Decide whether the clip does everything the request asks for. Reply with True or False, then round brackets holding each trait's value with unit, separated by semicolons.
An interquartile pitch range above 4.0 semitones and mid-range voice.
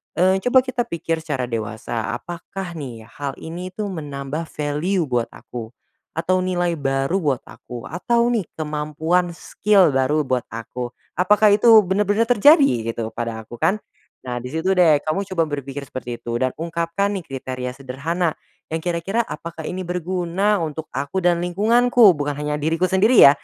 True (5.4 semitones; 165 Hz)